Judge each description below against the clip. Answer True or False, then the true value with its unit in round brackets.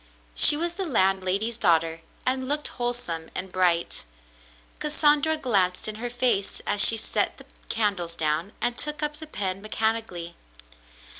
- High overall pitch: True (215 Hz)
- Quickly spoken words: False (145 wpm)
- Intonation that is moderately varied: False (6.1 semitones)